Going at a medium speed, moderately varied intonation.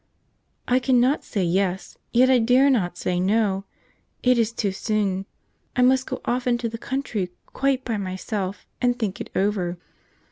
Yes: average, 165 wpm; average, 4.6 semitones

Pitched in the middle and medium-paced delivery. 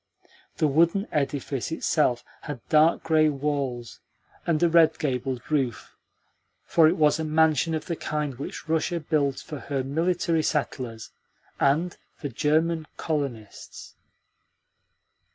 No: medium, 150 Hz; slow, 125 wpm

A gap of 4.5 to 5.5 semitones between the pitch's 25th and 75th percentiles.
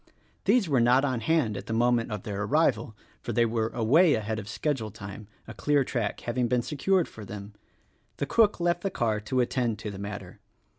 Yes: average, 4.9 semitones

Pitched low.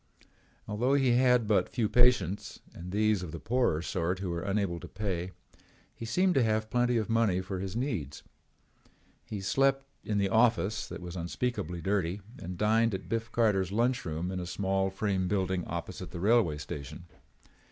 Yes: low, 100 Hz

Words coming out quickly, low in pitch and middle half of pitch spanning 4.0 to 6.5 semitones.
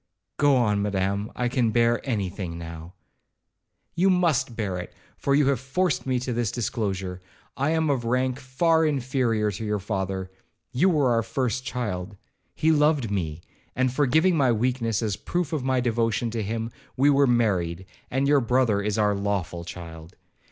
No: average, 175 wpm; low, 115 Hz; average, 4.9 semitones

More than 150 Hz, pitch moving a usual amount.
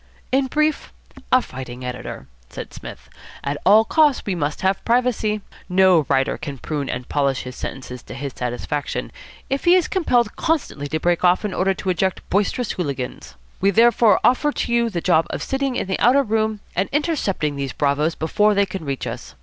No: high, 190 Hz; wide, 8.6 semitones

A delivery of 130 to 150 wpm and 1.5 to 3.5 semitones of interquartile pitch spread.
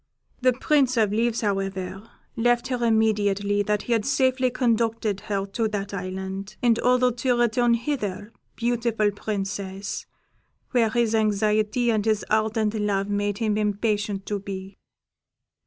Yes: average, 140 wpm; average, 2.8 semitones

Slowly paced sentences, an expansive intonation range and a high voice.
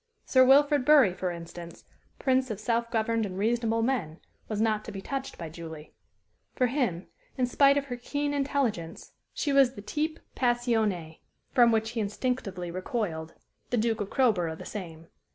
No: average, 170 wpm; wide, 5.9 semitones; high, 225 Hz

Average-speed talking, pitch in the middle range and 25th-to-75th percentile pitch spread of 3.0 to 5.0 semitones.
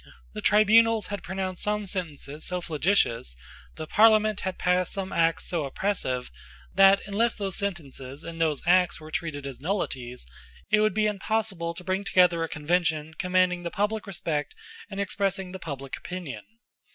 Yes: average, 160 wpm; medium, 180 Hz; average, 4.0 semitones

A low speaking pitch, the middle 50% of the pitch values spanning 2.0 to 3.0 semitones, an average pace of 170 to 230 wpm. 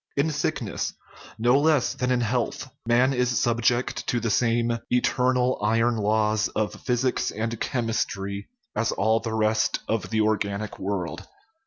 No: low, 115 Hz; narrow, 2.4 semitones; average, 145 wpm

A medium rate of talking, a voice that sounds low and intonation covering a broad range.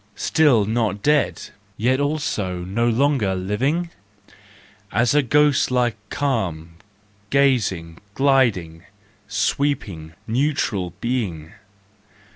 No: slow, 85 wpm; low, 120 Hz; wide, 6.8 semitones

